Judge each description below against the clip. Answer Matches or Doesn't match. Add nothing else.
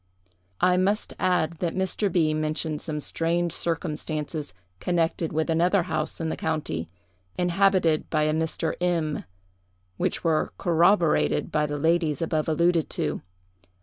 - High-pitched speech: Doesn't match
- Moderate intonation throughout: Doesn't match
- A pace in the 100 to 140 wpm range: Matches